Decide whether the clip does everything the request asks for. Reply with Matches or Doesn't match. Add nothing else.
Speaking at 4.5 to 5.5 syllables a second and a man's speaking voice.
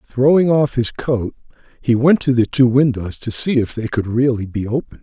Matches